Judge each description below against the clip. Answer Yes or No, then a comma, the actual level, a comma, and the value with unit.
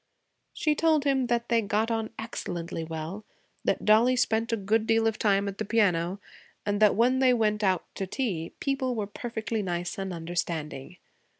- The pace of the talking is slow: No, average, 180 wpm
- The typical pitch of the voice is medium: No, high, 215 Hz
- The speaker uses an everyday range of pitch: Yes, average, 4.0 semitones